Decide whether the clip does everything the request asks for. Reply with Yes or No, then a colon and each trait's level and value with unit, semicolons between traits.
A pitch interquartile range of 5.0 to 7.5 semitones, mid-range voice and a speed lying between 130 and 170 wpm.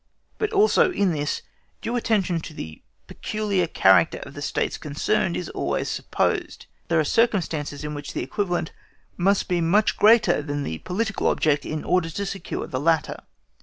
Yes: wide, 5.6 semitones; medium, 175 Hz; average, 165 wpm